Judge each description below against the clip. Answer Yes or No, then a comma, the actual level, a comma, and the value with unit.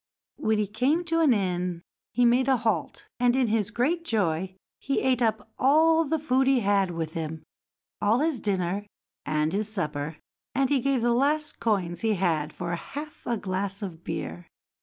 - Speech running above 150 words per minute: Yes, average, 180 wpm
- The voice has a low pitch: No, high, 220 Hz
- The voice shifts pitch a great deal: Yes, wide, 6.6 semitones